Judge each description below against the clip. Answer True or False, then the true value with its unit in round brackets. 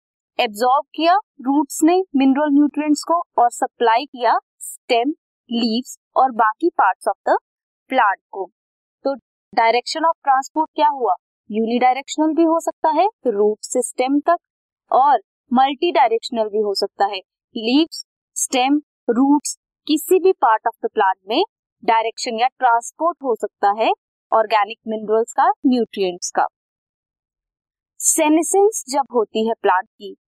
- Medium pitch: False (270 Hz)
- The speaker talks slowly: False (135 wpm)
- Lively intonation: True (6.2 semitones)